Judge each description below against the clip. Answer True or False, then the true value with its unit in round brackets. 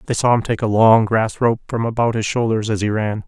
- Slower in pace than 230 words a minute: False (275 wpm)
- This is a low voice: True (110 Hz)